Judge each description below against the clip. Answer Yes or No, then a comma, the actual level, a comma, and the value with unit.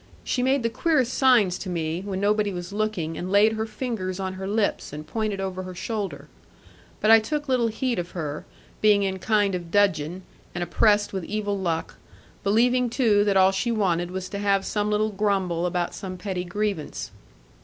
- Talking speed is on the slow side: No, average, 195 wpm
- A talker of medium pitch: No, high, 200 Hz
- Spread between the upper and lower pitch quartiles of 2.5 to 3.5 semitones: Yes, average, 2.9 semitones